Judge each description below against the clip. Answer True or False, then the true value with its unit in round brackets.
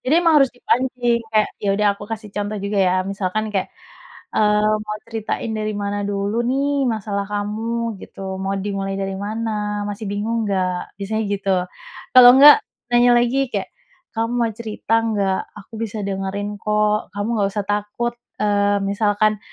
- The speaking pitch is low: False (210 Hz)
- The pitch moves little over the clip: True (2.2 semitones)